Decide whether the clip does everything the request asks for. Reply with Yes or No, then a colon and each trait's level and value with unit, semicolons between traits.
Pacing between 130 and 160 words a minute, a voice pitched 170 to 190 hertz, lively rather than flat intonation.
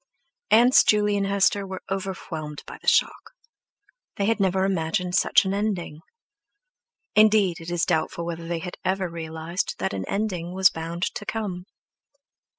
No: average, 155 wpm; medium, 185 Hz; average, 3.1 semitones